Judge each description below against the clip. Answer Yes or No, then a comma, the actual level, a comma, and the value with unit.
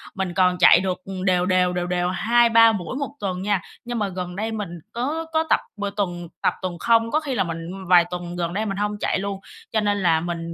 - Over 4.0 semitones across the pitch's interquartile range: No, average, 3.5 semitones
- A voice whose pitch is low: No, high, 190 Hz